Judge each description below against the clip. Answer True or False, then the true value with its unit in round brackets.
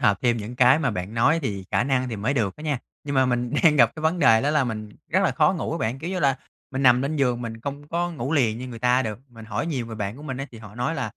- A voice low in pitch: True (125 Hz)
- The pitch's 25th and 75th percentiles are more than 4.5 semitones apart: False (3.9 semitones)